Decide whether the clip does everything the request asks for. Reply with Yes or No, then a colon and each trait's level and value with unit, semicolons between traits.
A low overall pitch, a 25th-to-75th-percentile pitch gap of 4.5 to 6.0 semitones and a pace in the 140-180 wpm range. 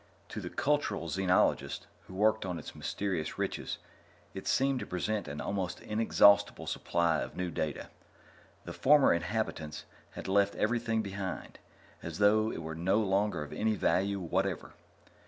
No: low, 100 Hz; average, 3.8 semitones; average, 150 wpm